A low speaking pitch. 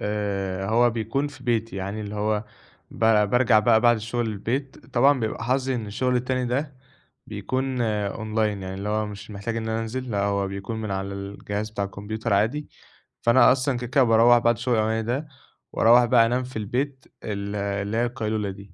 Yes: low, 110 Hz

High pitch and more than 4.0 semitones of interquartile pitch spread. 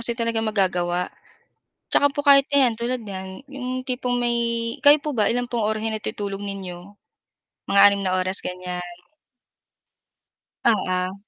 Yes: high, 215 Hz; average, 4.6 semitones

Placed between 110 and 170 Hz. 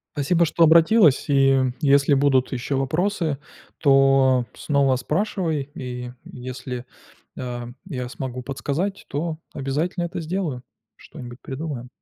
Yes: medium, 140 Hz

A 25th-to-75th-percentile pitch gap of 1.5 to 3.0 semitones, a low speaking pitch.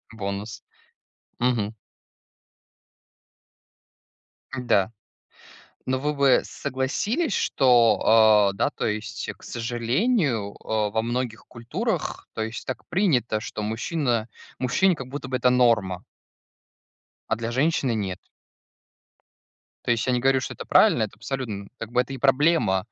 No: average, 3.4 semitones; low, 120 Hz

